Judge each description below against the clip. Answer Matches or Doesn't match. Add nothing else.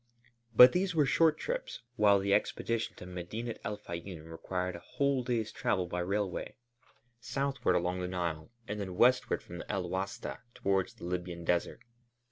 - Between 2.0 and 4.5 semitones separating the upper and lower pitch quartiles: Doesn't match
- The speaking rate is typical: Matches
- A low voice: Matches